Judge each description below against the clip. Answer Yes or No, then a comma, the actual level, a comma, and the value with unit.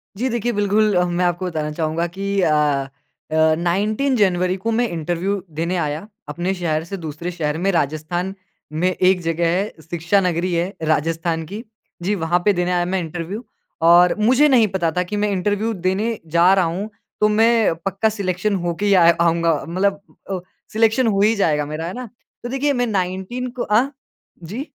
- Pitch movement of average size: Yes, average, 3.6 semitones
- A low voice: No, medium, 185 Hz